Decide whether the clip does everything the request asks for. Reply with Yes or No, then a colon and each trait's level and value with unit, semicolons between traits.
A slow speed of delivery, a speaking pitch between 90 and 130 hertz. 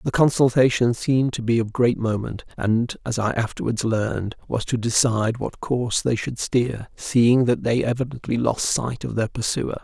No: average, 185 wpm; low, 120 Hz